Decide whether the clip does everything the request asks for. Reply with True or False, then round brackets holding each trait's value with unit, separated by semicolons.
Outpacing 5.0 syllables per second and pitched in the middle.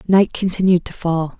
False (4.9 syllables/s; 180 Hz)